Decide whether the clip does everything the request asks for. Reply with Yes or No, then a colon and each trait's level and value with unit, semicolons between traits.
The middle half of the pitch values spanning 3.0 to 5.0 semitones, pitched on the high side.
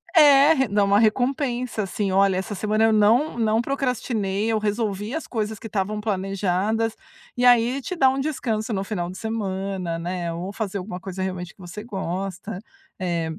Yes: average, 3.3 semitones; high, 210 Hz